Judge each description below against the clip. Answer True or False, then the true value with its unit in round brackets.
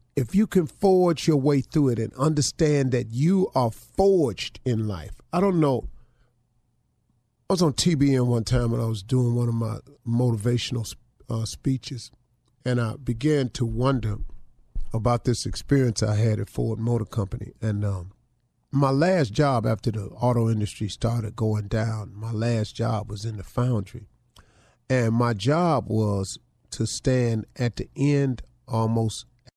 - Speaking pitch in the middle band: False (120 Hz)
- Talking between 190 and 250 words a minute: False (160 wpm)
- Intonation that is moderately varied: True (3.1 semitones)